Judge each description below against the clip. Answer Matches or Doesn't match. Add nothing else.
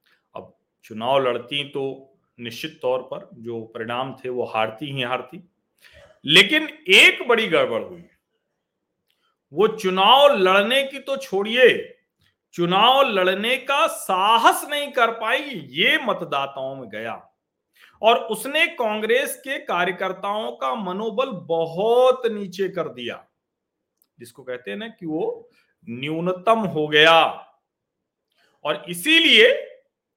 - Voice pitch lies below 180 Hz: Doesn't match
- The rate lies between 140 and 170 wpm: Doesn't match